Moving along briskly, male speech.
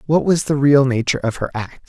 Yes: fast, 255 wpm; male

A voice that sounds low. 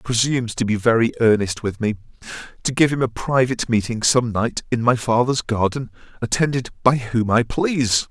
Yes: low, 120 Hz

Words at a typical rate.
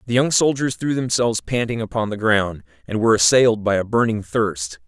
Yes: average, 195 wpm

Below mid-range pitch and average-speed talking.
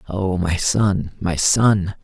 Yes: very low, 95 Hz; average, 145 wpm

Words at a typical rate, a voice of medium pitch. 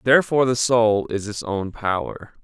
No: average, 170 wpm; low, 115 Hz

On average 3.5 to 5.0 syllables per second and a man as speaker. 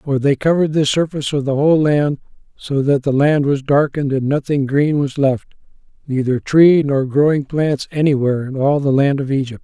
No: 5.4 syllables/s; male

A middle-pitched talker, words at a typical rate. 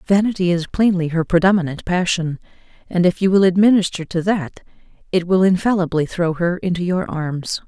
Yes: medium, 180 Hz; average, 165 wpm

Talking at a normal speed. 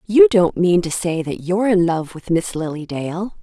No: fast, 230 wpm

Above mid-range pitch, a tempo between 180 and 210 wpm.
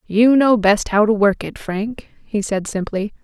Yes: high, 210 Hz; fast, 205 wpm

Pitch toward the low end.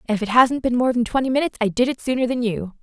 No: high, 240 Hz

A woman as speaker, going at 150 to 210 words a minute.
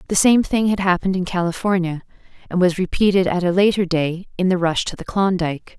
Yes: female; fast, 205 wpm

